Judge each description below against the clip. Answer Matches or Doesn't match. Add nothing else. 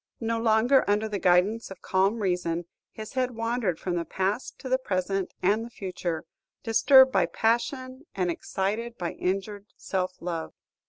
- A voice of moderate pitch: Doesn't match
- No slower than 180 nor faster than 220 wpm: Doesn't match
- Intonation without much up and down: Doesn't match